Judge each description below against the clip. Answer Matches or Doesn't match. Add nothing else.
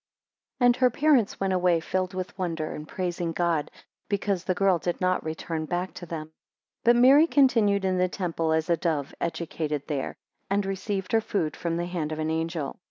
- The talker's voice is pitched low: Doesn't match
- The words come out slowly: Doesn't match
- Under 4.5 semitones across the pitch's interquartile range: Matches